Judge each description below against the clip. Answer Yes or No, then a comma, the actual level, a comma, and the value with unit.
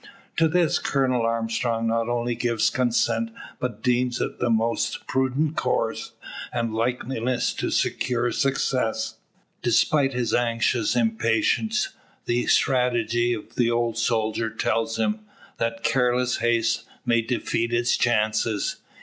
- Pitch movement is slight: Yes, narrow, 1.6 semitones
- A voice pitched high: No, low, 120 Hz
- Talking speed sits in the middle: No, slow, 125 wpm